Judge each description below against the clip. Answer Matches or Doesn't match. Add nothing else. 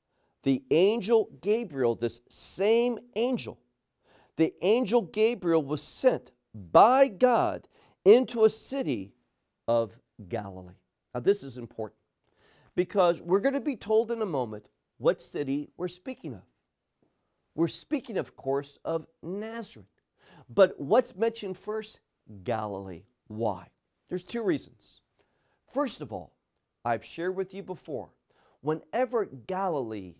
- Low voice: Doesn't match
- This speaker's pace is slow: Matches